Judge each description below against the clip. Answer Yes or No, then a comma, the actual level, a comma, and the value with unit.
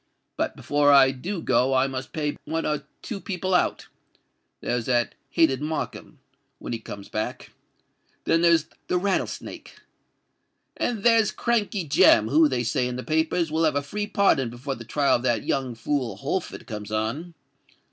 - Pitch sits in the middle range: Yes, medium, 145 Hz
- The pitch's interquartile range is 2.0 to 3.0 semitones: No, average, 5.2 semitones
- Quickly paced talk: No, average, 160 wpm